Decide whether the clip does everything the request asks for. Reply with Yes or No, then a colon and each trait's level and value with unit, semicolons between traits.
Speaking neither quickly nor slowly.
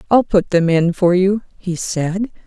Yes: average, 195 wpm